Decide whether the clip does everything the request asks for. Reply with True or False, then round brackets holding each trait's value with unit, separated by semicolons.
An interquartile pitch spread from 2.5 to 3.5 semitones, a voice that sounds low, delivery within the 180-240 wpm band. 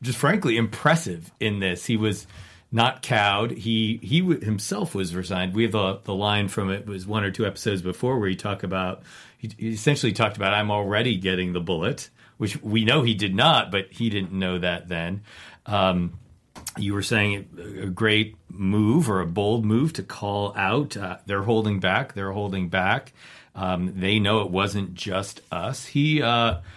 True (3.1 semitones; 100 Hz; 190 wpm)